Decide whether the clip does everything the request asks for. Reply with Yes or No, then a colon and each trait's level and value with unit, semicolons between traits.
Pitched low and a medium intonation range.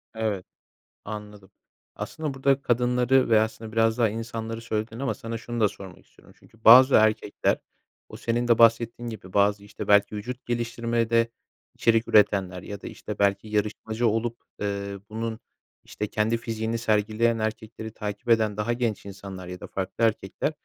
No: low, 110 Hz; narrow, 2.0 semitones